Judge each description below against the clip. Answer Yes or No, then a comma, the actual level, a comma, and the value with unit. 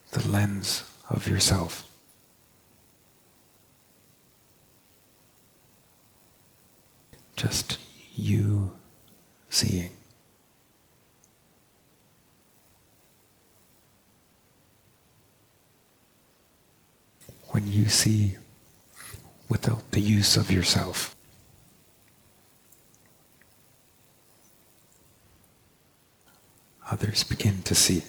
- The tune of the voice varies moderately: No, narrow, 2.0 semitones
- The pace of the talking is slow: Yes, slow, 40 wpm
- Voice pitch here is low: Yes, low, 105 Hz